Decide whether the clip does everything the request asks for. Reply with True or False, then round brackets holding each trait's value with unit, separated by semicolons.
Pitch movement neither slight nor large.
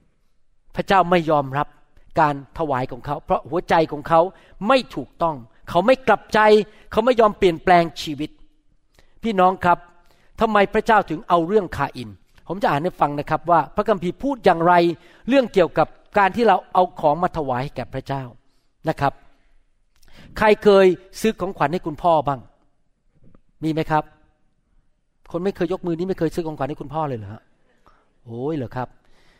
True (4.3 semitones)